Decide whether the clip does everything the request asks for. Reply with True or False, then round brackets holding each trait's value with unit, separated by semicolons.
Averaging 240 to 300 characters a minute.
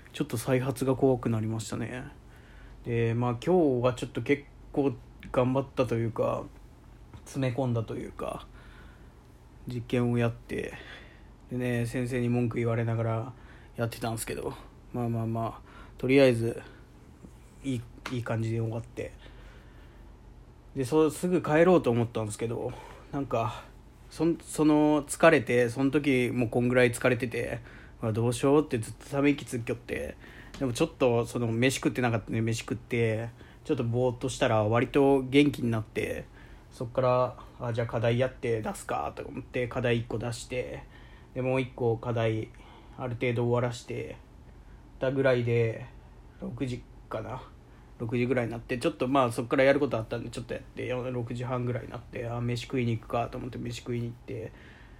False (335 characters per minute)